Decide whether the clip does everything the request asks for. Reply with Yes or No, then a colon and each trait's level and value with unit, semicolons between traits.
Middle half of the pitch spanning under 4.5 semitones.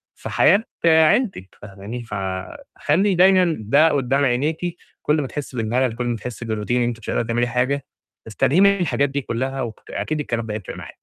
No: average, 5.1 semitones